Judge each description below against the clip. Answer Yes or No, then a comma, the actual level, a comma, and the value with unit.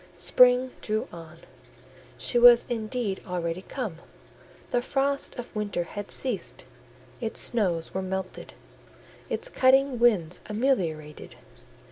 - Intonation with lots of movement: Yes, wide, 5.8 semitones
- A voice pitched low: No, high, 215 Hz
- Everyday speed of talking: No, slow, 110 wpm